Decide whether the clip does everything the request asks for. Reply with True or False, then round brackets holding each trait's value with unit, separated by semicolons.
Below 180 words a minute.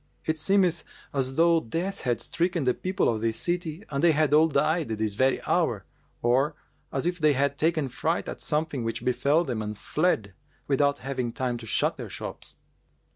False (185 wpm)